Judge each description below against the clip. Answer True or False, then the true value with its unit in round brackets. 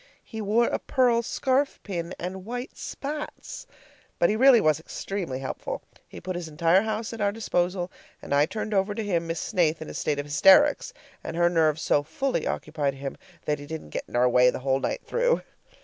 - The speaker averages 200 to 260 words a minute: True (205 wpm)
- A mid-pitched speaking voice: True (180 Hz)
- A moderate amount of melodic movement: False (6.3 semitones)